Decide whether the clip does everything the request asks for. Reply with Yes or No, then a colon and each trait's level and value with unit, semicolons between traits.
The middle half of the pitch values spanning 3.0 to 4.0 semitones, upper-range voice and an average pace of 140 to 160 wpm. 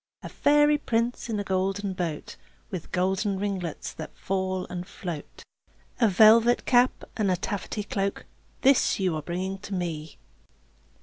Yes: average, 3.3 semitones; high, 195 Hz; average, 145 wpm